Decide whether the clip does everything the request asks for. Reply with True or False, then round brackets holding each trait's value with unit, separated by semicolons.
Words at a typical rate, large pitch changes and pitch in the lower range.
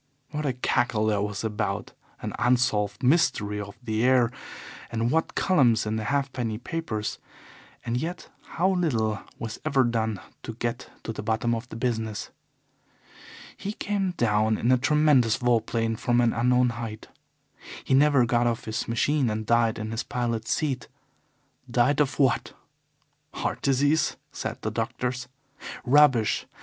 False (150 wpm; 3.4 semitones; 120 Hz)